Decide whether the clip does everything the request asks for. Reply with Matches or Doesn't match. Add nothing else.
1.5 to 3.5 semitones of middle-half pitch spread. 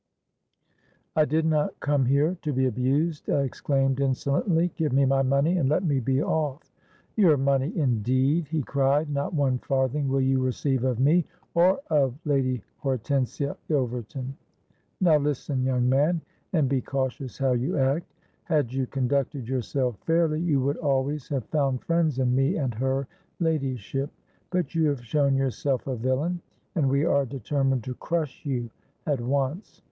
Matches